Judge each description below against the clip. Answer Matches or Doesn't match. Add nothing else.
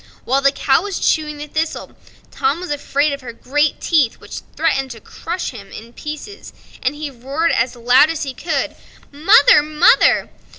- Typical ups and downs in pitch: Matches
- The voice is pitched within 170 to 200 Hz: Doesn't match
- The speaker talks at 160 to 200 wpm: Matches